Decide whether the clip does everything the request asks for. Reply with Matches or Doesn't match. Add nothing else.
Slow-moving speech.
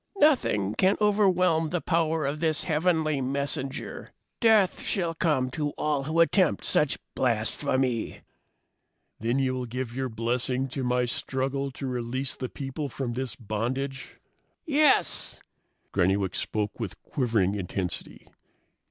Matches